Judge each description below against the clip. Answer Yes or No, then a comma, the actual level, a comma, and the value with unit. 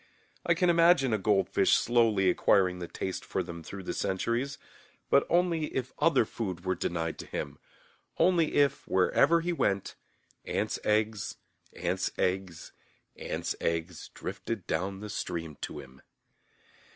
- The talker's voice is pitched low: Yes, low, 100 Hz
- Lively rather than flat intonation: Yes, wide, 7.2 semitones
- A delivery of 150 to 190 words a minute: No, average, 140 wpm